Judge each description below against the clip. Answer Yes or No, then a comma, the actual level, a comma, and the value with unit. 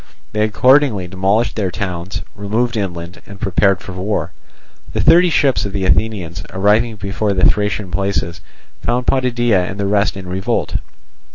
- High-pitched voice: No, low, 100 Hz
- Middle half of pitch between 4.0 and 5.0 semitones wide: No, average, 2.9 semitones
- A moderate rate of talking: Yes, average, 155 wpm